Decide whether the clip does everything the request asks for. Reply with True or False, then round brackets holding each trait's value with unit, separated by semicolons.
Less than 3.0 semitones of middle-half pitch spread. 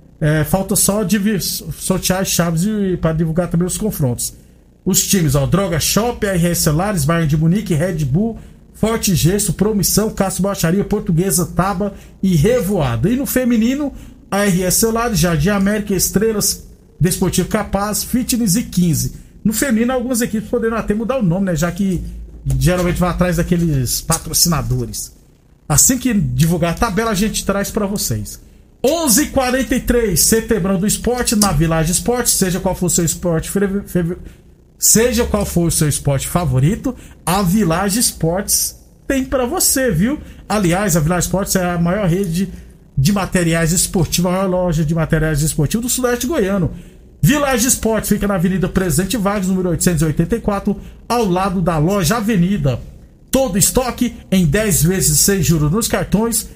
False (4.1 semitones)